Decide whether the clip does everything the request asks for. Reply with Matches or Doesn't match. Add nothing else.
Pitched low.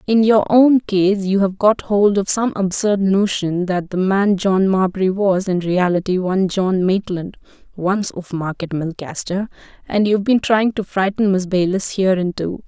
Doesn't match